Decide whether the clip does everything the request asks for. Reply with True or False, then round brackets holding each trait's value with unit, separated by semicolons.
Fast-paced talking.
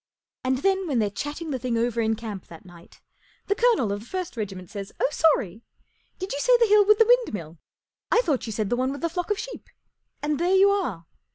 True (240 wpm)